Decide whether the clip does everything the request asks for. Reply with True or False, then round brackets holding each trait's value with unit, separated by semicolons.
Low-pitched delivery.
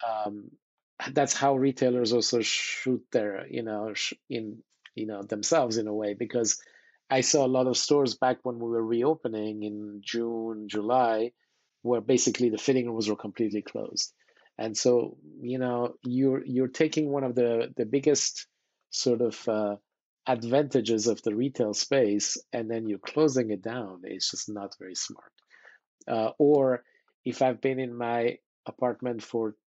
True (120 Hz)